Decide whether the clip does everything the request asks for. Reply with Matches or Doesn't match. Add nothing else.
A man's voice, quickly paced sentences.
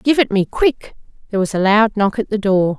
Doesn't match